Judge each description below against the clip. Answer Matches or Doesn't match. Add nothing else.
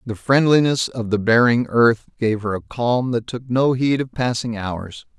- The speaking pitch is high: Doesn't match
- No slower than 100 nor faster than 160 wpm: Doesn't match